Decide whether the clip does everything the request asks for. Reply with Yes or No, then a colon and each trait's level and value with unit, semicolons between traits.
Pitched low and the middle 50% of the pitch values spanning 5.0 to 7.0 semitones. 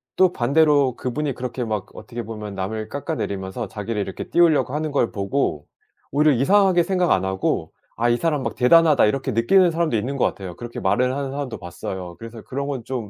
Yes: low, 125 Hz; wide, 5.6 semitones